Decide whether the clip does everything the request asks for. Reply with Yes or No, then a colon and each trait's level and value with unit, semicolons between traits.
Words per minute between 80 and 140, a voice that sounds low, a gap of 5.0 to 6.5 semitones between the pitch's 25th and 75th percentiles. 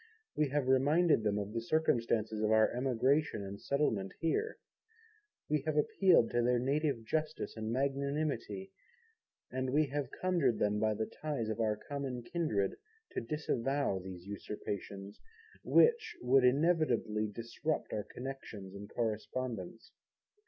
Yes: slow, 135 wpm; low, 125 Hz; wide, 5.5 semitones